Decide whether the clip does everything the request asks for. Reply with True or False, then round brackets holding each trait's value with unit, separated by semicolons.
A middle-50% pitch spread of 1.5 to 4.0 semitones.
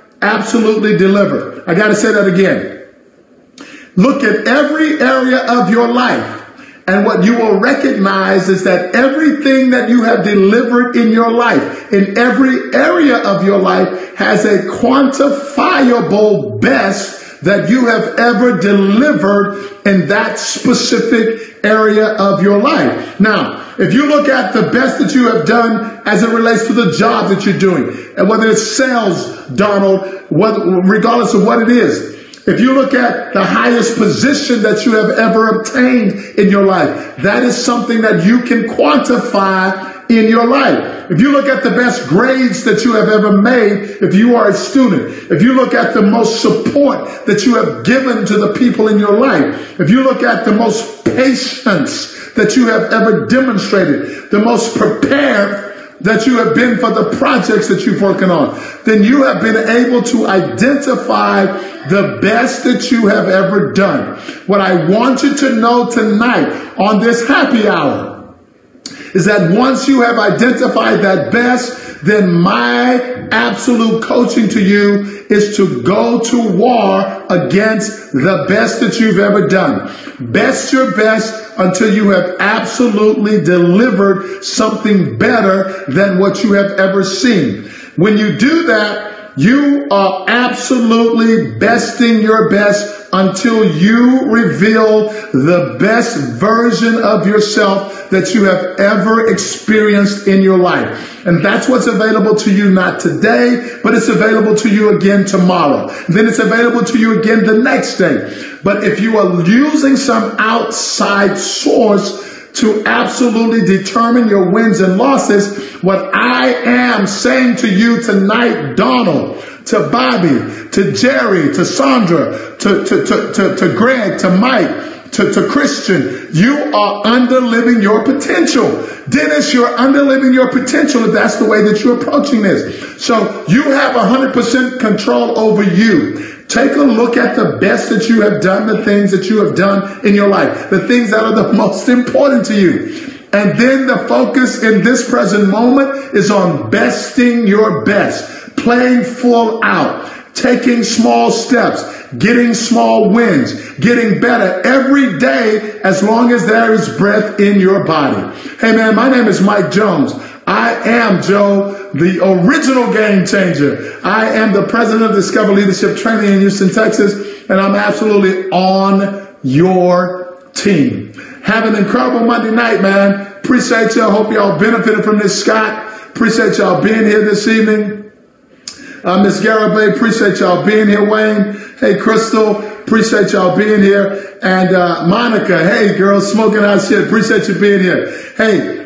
True (3.2 semitones)